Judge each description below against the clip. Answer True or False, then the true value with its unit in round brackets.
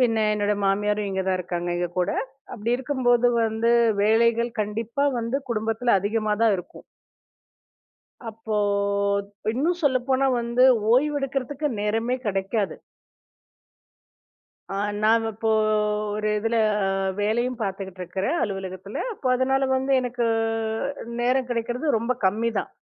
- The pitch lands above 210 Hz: True (230 Hz)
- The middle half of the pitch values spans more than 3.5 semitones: False (3.2 semitones)